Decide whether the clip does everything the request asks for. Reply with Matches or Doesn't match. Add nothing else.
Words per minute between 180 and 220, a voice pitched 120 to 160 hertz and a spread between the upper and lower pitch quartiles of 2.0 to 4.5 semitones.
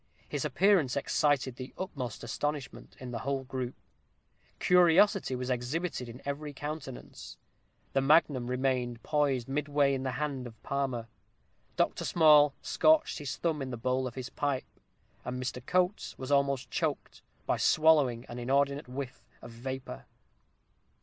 Doesn't match